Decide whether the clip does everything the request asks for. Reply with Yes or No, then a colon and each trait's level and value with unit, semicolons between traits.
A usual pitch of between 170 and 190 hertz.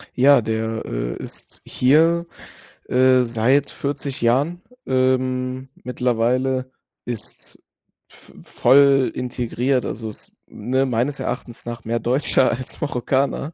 No: low, 130 Hz